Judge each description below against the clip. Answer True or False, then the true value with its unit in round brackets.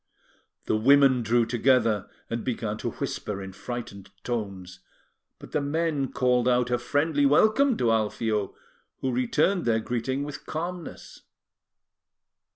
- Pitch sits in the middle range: False (125 Hz)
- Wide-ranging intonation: False (4.2 semitones)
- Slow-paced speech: True (130 wpm)